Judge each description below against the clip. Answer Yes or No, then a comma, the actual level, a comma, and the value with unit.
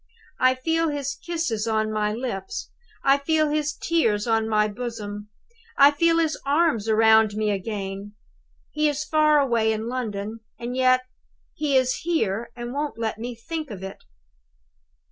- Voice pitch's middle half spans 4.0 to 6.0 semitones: Yes, average, 5.3 semitones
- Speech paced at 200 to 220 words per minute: No, average, 155 wpm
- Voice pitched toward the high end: Yes, high, 240 Hz